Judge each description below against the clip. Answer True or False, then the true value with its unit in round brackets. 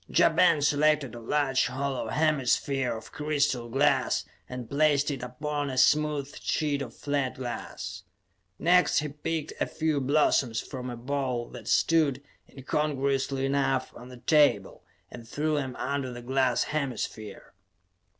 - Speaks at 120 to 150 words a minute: True (140 wpm)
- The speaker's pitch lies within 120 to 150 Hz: True (140 Hz)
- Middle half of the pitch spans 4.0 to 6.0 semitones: False (2.9 semitones)